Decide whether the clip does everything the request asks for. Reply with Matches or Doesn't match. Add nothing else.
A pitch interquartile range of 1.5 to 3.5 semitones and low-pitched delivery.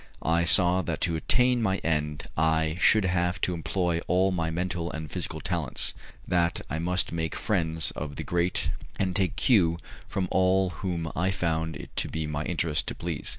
Matches